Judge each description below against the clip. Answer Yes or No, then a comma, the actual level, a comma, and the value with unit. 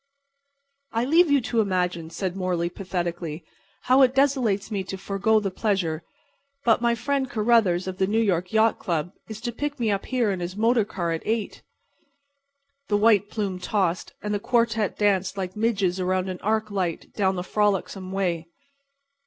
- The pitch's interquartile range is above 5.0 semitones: No, average, 3.6 semitones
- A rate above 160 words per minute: Yes, average, 175 wpm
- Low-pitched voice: No, high, 200 Hz